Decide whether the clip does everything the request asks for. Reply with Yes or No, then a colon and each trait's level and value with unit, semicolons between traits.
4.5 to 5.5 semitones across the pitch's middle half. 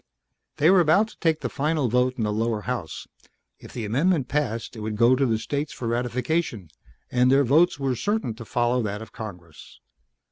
Yes: average, 4.8 semitones